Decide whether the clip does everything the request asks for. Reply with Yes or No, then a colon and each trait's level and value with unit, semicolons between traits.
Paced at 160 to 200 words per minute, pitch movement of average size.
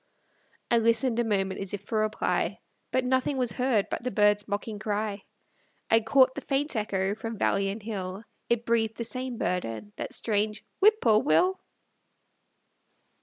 Yes: average, 165 wpm; average, 3.2 semitones